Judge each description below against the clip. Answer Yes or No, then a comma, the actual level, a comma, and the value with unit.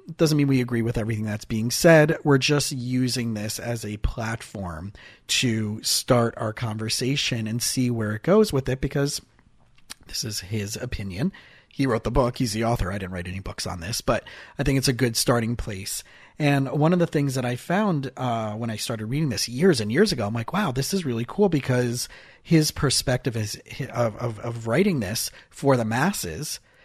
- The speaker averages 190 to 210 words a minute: Yes, fast, 205 wpm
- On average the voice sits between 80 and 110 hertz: No, low, 120 Hz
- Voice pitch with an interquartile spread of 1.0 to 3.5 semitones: No, average, 4.2 semitones